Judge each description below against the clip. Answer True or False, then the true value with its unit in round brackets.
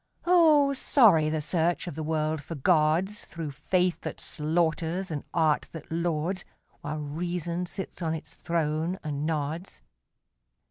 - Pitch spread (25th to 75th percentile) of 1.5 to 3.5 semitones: True (2.6 semitones)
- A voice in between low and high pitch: True (165 Hz)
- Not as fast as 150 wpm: True (140 wpm)